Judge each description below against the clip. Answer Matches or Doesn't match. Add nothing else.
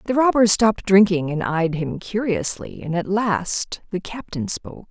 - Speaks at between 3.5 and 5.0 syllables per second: Matches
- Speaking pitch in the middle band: Doesn't match